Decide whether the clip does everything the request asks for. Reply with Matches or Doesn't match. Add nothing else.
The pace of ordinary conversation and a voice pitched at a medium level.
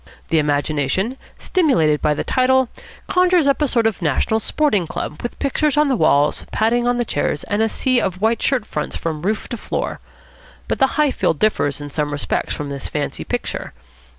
Doesn't match